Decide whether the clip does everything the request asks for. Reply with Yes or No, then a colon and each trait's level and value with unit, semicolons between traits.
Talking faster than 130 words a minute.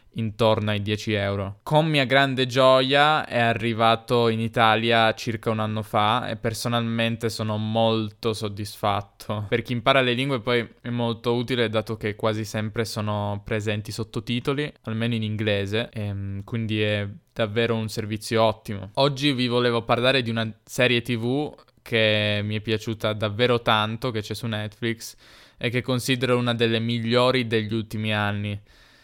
Yes: average, 150 wpm